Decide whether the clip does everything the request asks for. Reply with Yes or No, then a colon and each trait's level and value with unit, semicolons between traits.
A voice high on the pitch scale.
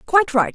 Yes: very high, 280 Hz